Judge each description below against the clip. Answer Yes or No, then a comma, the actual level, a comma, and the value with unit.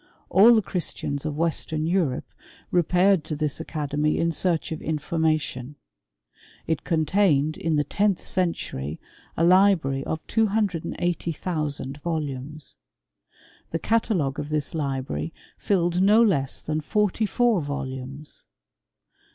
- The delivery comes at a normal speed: No, slow, 120 wpm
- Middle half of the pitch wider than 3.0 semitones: Yes, average, 4.0 semitones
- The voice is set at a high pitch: No, medium, 160 Hz